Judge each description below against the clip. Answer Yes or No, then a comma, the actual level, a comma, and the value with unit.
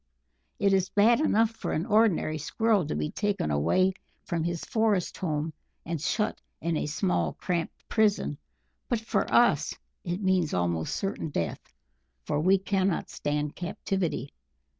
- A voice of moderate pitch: Yes, medium, 180 Hz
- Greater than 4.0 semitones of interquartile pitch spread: Yes, wide, 5.4 semitones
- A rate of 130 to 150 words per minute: Yes, average, 145 wpm